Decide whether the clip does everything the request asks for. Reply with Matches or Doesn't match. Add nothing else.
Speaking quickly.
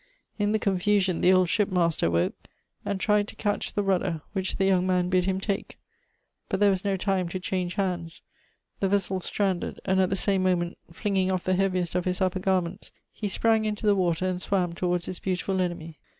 Matches